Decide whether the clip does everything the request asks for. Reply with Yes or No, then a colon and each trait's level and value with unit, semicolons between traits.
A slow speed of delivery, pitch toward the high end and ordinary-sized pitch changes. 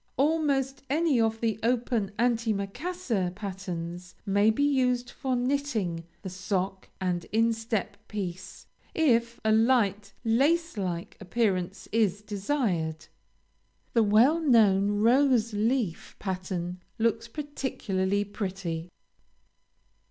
Yes: slow, 105 wpm; high, 220 Hz; average, 4.5 semitones